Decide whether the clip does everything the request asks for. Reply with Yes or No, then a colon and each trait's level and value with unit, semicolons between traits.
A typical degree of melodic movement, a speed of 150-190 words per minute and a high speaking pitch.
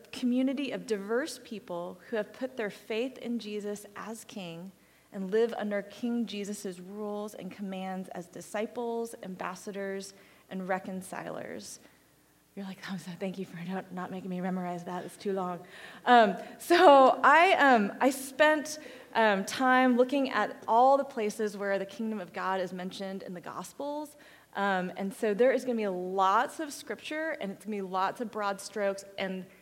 Yes: average, 4.2 semitones; average, 175 wpm; high, 205 Hz